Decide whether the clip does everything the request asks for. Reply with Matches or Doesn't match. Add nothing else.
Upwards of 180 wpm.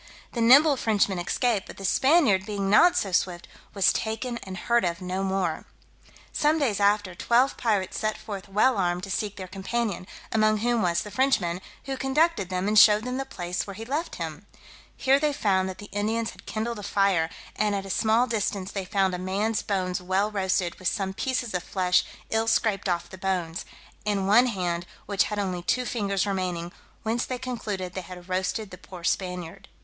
Matches